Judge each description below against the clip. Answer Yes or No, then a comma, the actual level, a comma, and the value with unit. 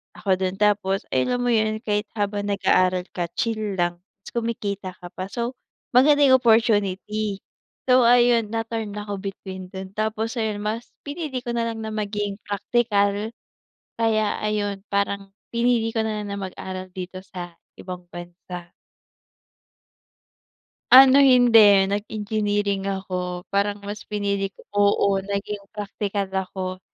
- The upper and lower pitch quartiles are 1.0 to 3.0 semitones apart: Yes, narrow, 2.6 semitones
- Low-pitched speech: No, high, 205 Hz